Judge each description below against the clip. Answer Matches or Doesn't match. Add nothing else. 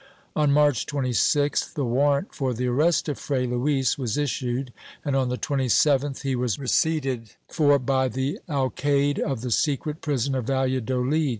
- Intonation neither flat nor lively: Doesn't match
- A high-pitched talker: Doesn't match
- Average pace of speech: Matches